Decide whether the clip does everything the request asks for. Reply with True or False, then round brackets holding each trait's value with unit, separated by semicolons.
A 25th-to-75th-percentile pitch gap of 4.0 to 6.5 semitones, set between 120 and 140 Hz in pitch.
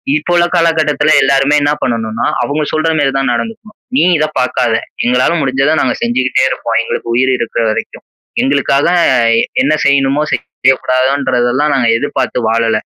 False (3.2 semitones; 135 Hz)